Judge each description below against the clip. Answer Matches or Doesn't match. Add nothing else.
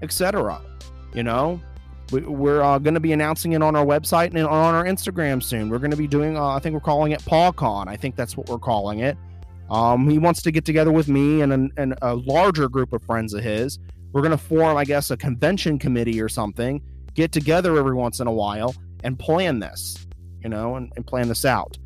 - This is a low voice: Matches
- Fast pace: Matches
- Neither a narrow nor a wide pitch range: Doesn't match